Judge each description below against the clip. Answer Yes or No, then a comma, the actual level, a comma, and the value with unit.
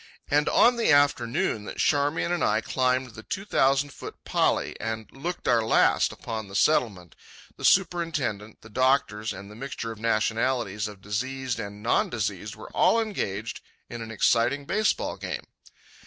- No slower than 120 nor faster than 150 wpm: No, average, 165 wpm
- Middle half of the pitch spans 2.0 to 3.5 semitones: No, average, 4.9 semitones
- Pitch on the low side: Yes, low, 120 Hz